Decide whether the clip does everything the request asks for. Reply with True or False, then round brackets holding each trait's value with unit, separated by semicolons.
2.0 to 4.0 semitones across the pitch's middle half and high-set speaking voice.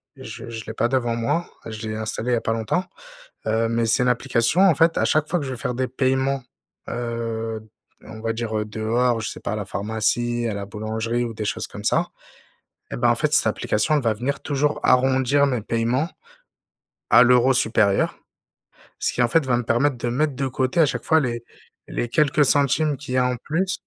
False (3.3 semitones; 120 Hz)